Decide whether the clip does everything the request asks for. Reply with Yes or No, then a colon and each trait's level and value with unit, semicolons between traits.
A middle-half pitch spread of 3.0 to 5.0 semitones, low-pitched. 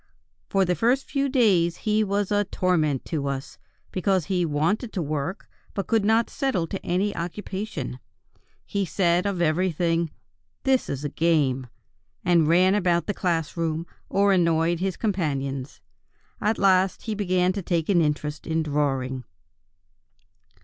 No: average, 4.2 semitones; medium, 175 Hz